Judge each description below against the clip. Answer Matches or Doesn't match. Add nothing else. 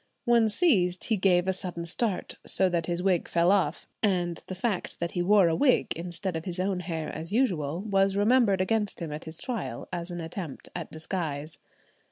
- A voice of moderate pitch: Matches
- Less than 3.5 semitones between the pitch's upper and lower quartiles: Matches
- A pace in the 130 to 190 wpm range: Doesn't match